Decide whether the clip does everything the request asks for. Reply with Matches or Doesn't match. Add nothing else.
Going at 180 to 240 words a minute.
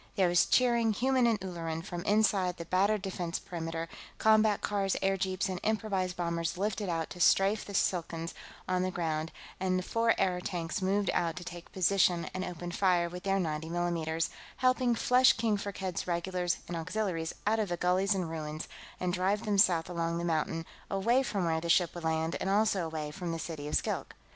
Matches